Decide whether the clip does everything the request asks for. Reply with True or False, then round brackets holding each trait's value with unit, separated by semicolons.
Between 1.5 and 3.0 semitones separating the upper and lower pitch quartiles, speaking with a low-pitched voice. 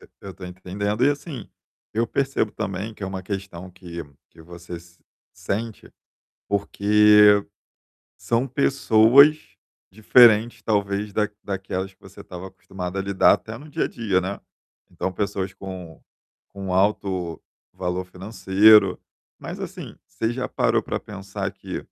True (2.6 semitones; 100 Hz)